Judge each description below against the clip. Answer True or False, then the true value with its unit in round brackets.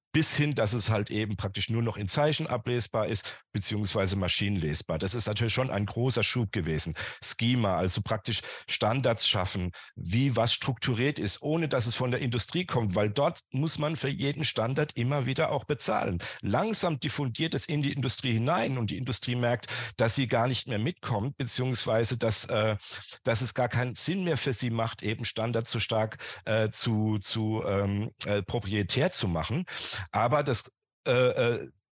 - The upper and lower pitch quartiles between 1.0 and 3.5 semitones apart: False (4.2 semitones)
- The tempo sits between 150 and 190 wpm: True (180 wpm)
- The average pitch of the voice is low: True (120 Hz)